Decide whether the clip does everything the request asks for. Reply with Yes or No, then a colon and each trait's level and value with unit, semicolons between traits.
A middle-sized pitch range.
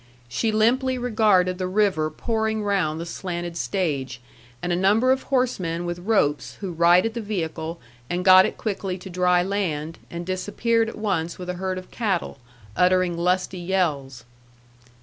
Yes: average, 3.6 semitones